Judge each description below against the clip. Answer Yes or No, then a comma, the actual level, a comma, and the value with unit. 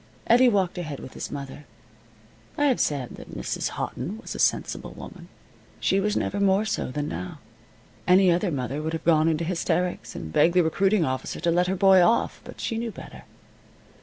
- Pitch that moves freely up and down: No, average, 4.7 semitones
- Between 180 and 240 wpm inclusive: Yes, average, 190 wpm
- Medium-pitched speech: Yes, medium, 175 Hz